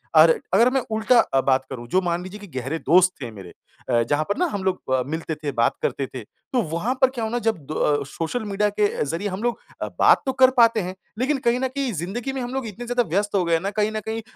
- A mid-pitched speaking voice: No, high, 200 Hz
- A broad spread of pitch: Yes, wide, 7.1 semitones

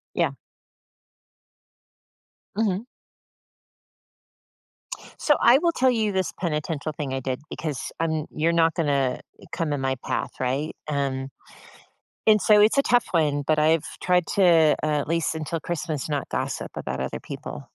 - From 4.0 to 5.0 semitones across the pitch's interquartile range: Yes, average, 4.3 semitones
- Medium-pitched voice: Yes, medium, 160 Hz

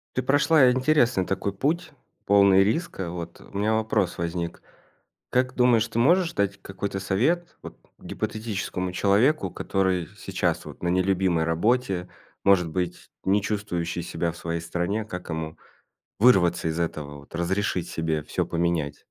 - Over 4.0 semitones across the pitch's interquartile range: Yes, average, 4.5 semitones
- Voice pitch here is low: Yes, very low, 95 Hz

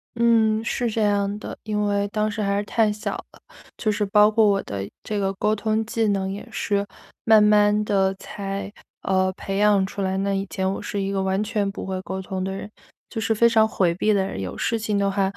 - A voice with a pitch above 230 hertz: No, high, 205 Hz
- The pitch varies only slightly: Yes, narrow, 1.7 semitones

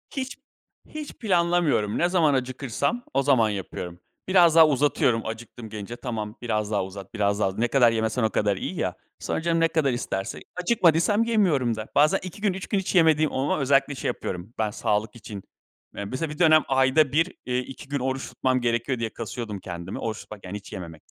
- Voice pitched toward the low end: Yes, low, 130 Hz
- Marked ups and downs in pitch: Yes, wide, 6.9 semitones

